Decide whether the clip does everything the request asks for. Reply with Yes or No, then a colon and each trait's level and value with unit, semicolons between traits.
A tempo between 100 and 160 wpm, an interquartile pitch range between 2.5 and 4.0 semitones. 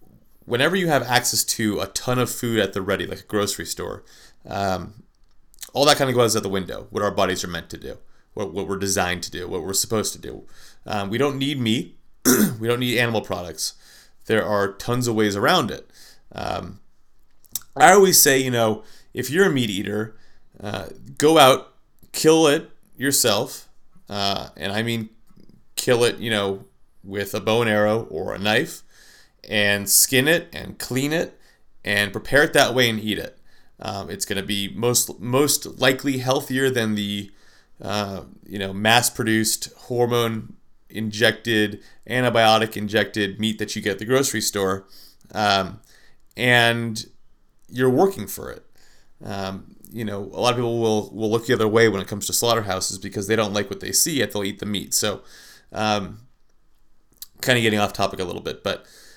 No: average, 185 wpm; average, 3.3 semitones